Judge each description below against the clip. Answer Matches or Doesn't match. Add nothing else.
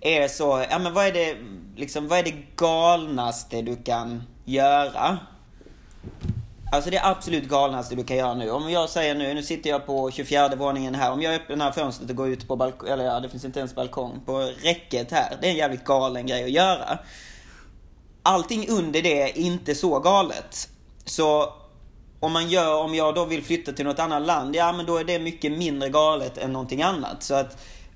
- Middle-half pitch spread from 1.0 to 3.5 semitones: Doesn't match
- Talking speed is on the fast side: Matches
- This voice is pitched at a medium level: Matches